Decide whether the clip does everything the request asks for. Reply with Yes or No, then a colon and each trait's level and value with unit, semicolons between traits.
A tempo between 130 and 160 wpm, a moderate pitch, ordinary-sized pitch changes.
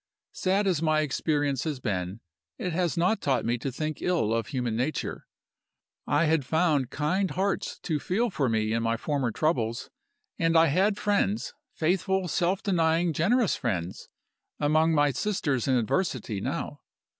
No: average, 155 wpm; medium, 155 Hz; wide, 6.2 semitones